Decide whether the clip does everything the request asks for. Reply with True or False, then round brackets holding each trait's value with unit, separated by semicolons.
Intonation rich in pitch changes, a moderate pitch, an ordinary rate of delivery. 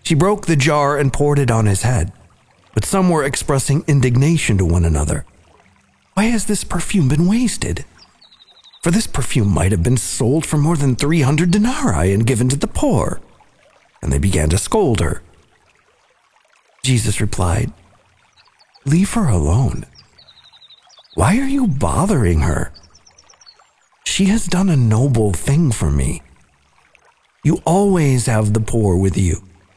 False (9.0 semitones; 125 Hz; 145 wpm)